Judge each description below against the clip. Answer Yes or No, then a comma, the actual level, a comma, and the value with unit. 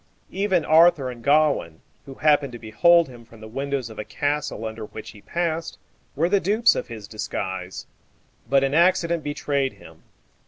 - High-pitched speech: No, medium, 140 Hz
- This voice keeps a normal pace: Yes, average, 170 wpm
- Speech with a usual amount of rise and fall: No, wide, 6.6 semitones